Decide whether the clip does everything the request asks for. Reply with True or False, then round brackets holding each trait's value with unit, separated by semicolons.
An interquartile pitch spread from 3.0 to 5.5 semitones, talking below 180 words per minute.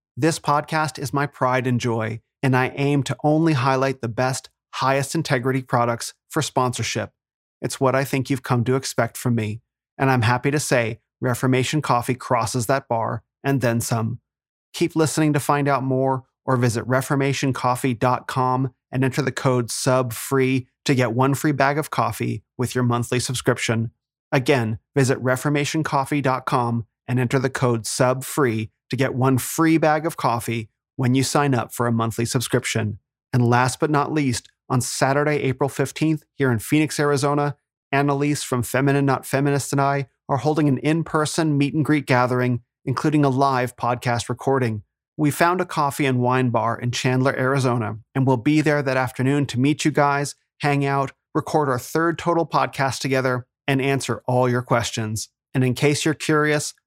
False (2.5 semitones; 170 wpm)